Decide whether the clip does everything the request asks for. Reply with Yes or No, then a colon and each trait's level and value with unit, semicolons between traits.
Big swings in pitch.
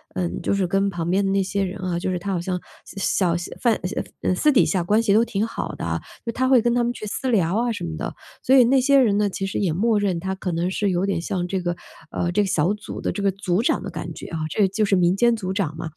No: average, 3.4 semitones